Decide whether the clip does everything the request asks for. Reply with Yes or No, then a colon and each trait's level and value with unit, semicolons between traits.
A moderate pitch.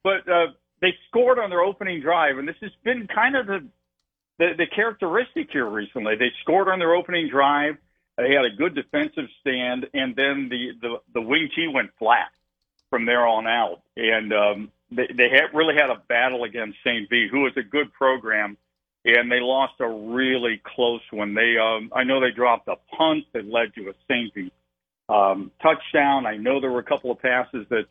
No: low, 130 Hz